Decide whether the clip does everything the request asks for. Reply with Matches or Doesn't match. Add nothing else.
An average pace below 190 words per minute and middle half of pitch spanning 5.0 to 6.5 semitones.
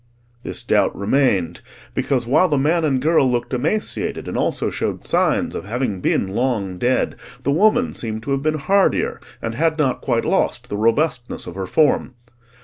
Matches